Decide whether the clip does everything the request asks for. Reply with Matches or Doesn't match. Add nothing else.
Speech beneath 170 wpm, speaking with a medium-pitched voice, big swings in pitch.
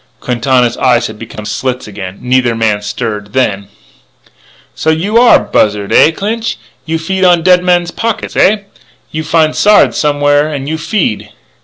Matches